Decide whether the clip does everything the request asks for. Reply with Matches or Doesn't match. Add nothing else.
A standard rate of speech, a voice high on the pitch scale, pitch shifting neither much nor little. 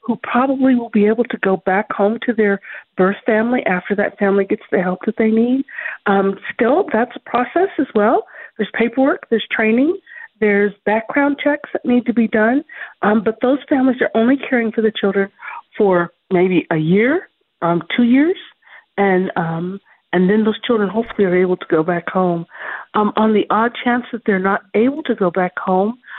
Matches